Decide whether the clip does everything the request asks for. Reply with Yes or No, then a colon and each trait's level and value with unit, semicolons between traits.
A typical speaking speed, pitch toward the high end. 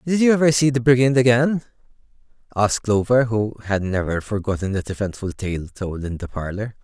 No: average, 175 wpm; low, 115 Hz